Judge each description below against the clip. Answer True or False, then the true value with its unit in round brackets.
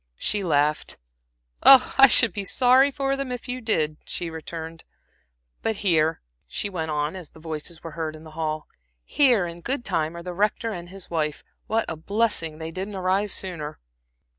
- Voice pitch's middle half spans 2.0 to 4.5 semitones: False (5.6 semitones)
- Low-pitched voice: False (175 Hz)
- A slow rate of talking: False (175 wpm)